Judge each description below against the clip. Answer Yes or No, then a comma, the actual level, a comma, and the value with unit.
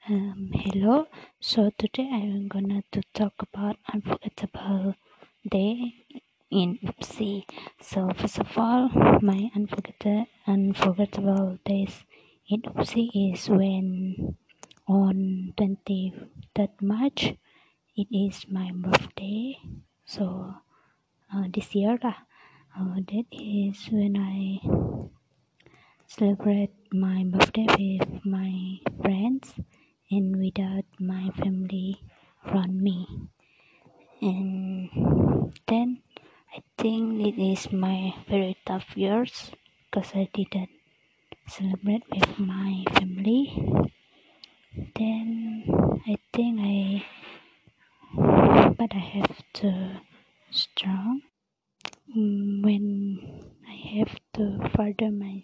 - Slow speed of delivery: Yes, slow, 90 wpm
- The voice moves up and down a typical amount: No, narrow, 1.8 semitones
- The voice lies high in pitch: Yes, high, 200 Hz